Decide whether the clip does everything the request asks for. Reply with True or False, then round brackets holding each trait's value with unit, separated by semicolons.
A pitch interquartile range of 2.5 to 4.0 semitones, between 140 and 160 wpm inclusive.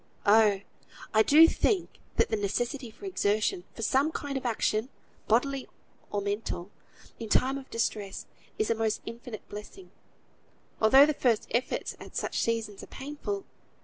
False (4.4 semitones; 150 wpm)